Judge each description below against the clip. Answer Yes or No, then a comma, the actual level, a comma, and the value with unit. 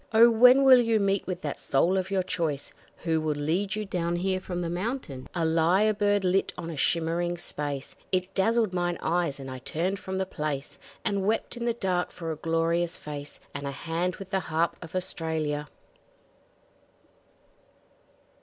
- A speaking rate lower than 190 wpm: Yes, average, 180 wpm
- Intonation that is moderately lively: Yes, average, 3.3 semitones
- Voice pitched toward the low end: No, medium, 175 Hz